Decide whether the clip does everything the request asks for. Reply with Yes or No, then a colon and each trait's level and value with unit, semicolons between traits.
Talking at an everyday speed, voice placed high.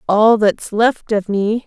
Yes: average, 180 wpm; high, 215 Hz